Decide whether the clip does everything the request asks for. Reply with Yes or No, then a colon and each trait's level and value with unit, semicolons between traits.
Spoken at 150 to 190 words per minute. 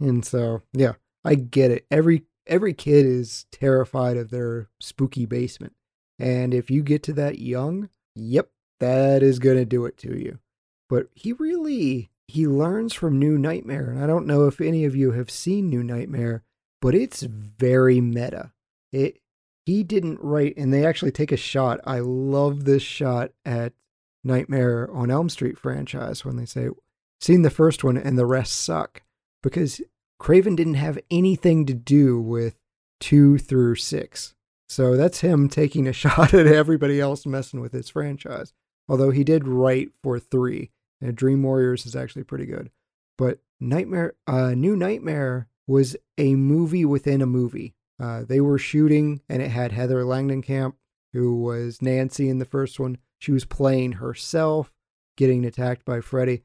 Yes: average, 170 wpm